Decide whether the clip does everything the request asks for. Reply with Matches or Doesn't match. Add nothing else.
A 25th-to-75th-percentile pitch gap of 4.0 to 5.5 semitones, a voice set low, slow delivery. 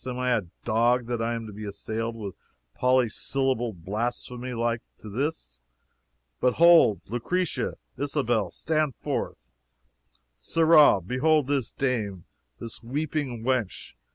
Doesn't match